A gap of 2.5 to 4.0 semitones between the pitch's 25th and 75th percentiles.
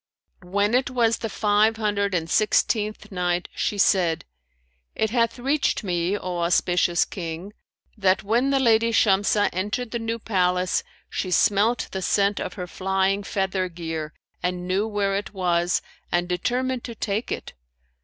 Yes: average, 3.6 semitones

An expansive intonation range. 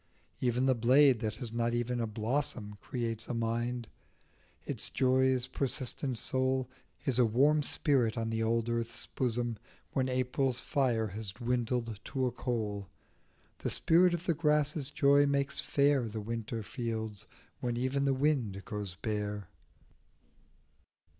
No: average, 2.9 semitones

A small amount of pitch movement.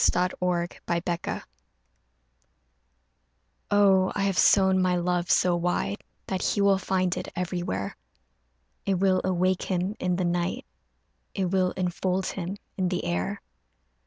Yes: narrow, 1.3 semitones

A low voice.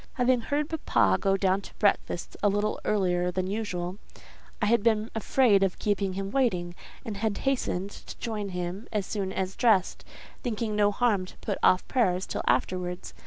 No: high, 200 Hz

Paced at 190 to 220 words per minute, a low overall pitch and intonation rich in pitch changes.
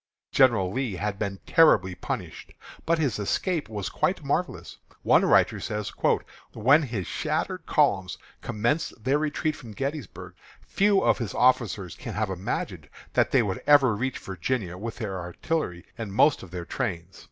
No: average, 155 wpm; low, 110 Hz; wide, 6.2 semitones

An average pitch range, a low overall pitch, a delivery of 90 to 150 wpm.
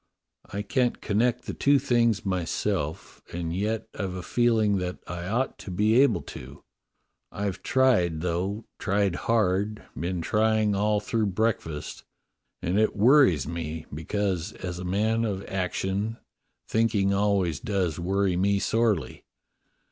Yes: average, 3.6 semitones; low, 100 Hz; slow, 135 wpm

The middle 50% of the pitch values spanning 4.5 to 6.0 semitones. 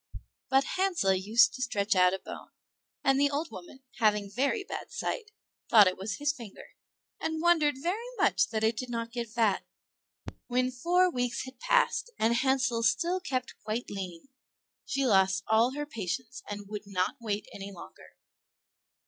Yes: wide, 5.5 semitones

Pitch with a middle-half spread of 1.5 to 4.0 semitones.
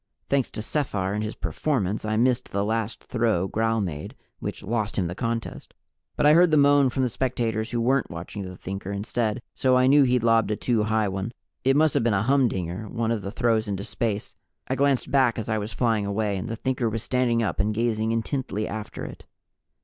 Yes: average, 3.3 semitones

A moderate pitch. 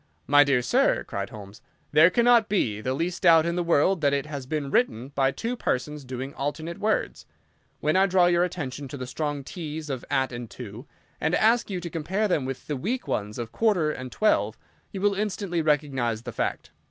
Yes: medium, 150 Hz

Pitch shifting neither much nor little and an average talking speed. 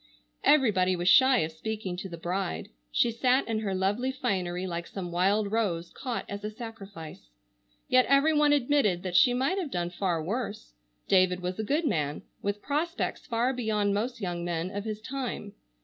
No: wide, 5.7 semitones; average, 180 wpm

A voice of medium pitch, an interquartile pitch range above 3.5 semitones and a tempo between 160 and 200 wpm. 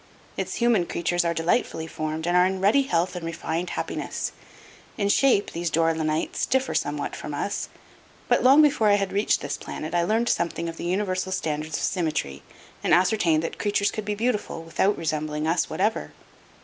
Yes: medium, 175 Hz; average, 4.1 semitones; average, 185 wpm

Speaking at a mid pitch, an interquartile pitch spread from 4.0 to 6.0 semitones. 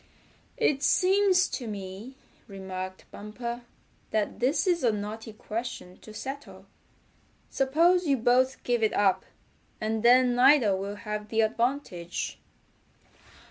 No: high, 235 Hz; average, 4.3 semitones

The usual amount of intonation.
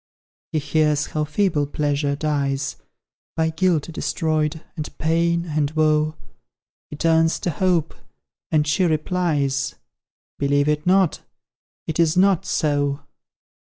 No: narrow, 2.0 semitones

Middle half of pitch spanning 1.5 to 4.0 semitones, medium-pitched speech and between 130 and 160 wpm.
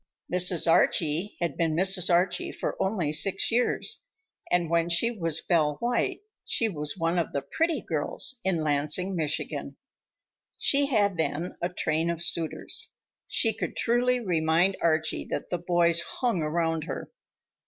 Yes: average, 3.4 semitones; medium, 170 Hz; average, 150 wpm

